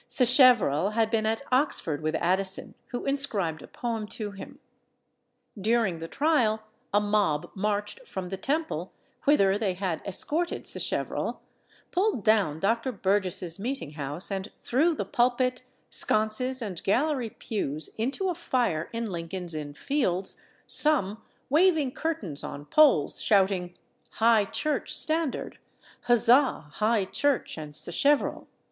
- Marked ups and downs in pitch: Yes, wide, 5.8 semitones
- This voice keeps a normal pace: No, slow, 130 wpm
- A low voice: No, high, 215 Hz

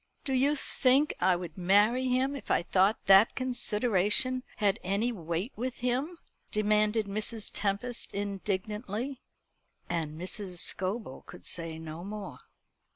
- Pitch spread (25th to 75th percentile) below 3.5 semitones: No, average, 4.8 semitones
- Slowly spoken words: Yes, slow, 130 wpm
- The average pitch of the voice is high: Yes, high, 210 Hz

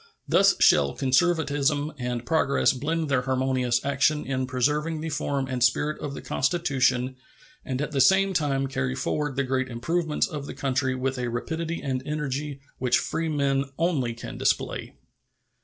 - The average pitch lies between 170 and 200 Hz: No, low, 135 Hz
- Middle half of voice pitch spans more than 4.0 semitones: No, average, 2.9 semitones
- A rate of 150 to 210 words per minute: Yes, average, 155 wpm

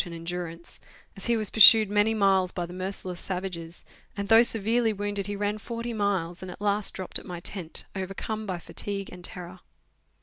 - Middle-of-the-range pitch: No, high, 195 Hz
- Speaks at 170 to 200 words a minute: Yes, average, 190 wpm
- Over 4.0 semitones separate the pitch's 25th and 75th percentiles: No, average, 2.7 semitones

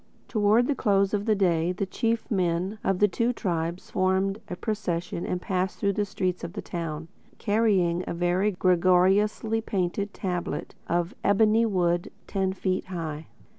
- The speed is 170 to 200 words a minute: No, average, 160 wpm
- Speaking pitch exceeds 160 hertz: Yes, high, 190 Hz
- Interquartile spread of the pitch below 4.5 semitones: Yes, average, 2.9 semitones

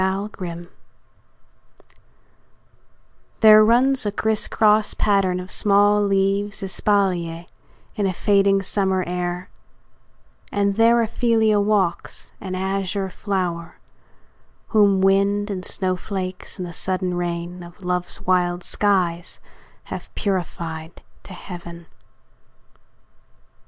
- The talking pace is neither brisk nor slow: No, slow, 95 wpm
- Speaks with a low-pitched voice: No, high, 195 Hz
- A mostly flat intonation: Yes, narrow, 2.3 semitones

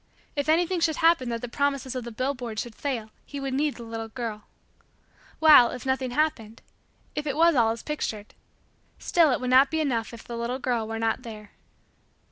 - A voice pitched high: Yes, very high, 255 Hz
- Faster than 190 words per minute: Yes, average, 200 wpm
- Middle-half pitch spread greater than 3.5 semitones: Yes, average, 3.9 semitones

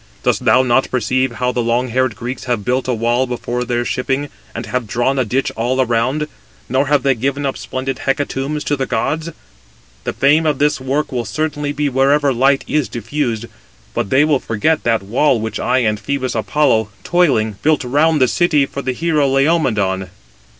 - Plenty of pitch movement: No, average, 3.3 semitones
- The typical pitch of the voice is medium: No, low, 130 Hz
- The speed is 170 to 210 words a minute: Yes, average, 185 wpm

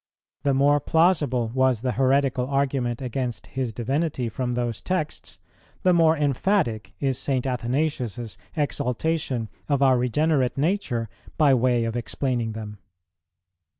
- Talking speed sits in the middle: No, slow, 125 wpm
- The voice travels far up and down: No, average, 3.3 semitones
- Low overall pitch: Yes, low, 130 Hz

